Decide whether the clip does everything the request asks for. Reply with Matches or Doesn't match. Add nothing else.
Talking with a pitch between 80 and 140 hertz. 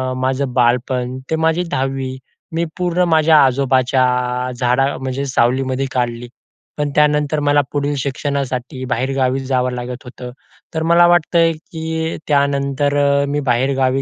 Matches